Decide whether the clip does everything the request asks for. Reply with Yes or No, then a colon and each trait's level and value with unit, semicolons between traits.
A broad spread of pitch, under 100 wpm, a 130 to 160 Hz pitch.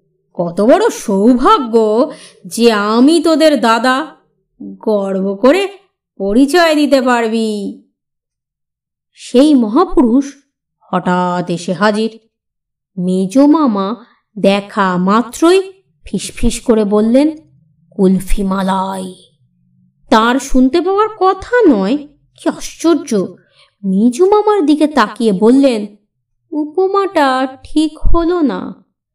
No: wide, 7.5 semitones; average, 85 wpm; high, 235 Hz